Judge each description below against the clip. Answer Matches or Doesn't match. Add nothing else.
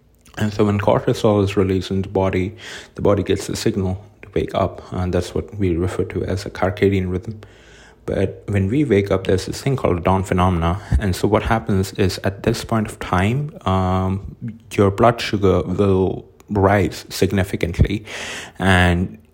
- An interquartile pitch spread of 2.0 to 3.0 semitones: Matches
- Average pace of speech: Matches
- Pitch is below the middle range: Matches